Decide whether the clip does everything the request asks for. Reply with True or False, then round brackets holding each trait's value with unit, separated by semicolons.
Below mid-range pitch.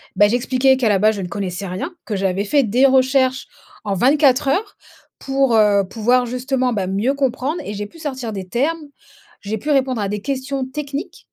False (255 Hz)